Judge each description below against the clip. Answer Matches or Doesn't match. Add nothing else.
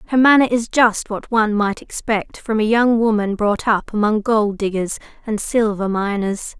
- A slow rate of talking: Doesn't match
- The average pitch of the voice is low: Doesn't match